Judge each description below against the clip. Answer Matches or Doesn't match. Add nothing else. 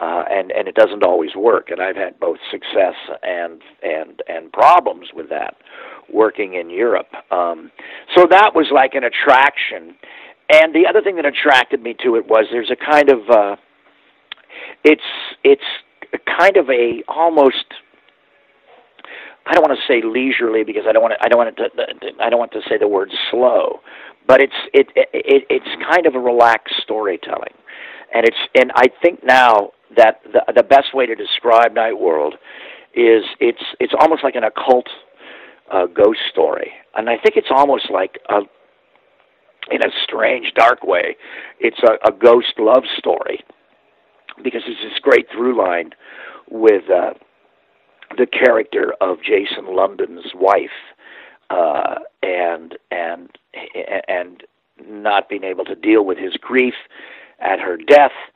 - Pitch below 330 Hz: Doesn't match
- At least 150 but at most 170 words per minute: Matches